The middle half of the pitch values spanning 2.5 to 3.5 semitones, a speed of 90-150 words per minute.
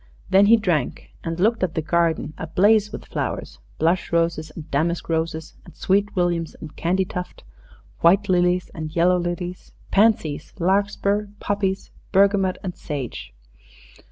Yes: average, 3.1 semitones; slow, 135 wpm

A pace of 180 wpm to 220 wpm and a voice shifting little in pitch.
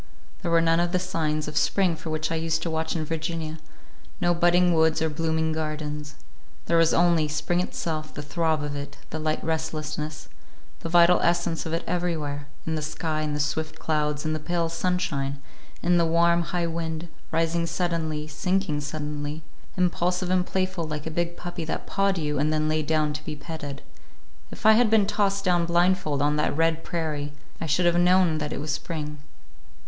Yes: average, 190 wpm; narrow, 2.1 semitones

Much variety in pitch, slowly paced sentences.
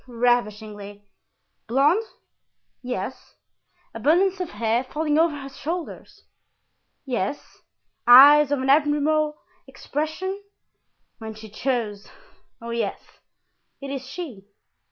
No: average, 4.8 semitones; slow, 95 wpm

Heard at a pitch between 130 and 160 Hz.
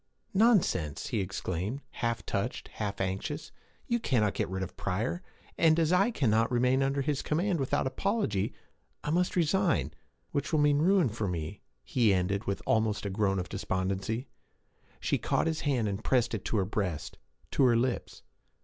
No: low, 115 Hz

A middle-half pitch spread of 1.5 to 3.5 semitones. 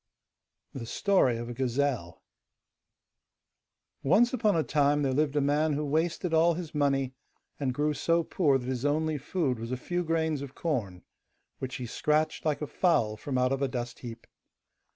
No: average, 3.9 semitones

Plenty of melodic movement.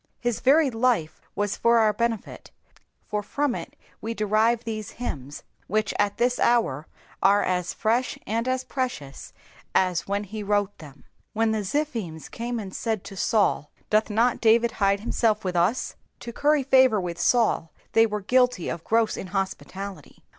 No: average, 3.4 semitones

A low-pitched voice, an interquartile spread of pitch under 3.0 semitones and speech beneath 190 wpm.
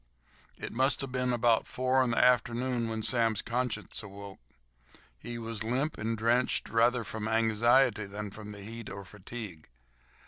Yes: low, 115 Hz; narrow, 2.6 semitones; average, 150 wpm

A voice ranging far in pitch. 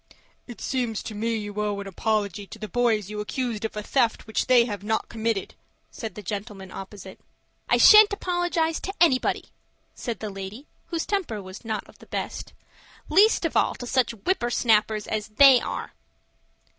No: average, 3.7 semitones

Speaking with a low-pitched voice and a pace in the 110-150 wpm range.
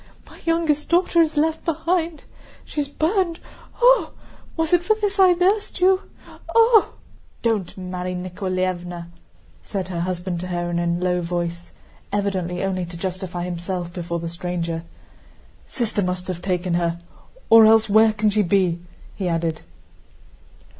No: medium, 185 Hz; average, 145 wpm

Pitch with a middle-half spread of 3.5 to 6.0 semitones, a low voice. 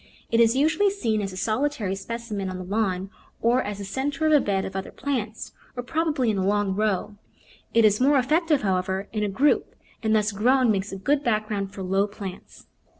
No: average, 4.8 semitones; high, 215 Hz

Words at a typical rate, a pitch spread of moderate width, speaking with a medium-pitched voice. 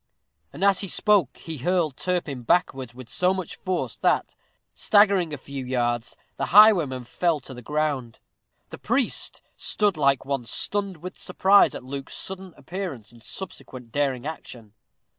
No: average, 155 wpm; wide, 6.4 semitones; medium, 150 Hz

